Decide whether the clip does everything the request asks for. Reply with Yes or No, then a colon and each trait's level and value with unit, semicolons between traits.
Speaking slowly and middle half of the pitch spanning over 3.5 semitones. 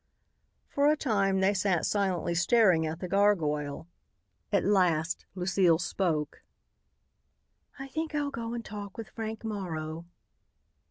Yes: slow, 125 wpm; average, 4.7 semitones